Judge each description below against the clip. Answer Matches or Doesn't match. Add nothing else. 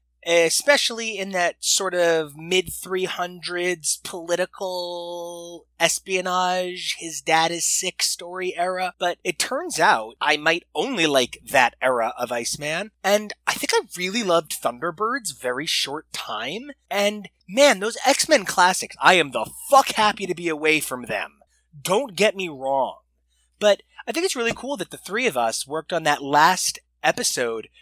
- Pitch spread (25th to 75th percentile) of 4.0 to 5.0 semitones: Matches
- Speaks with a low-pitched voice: Doesn't match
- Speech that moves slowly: Doesn't match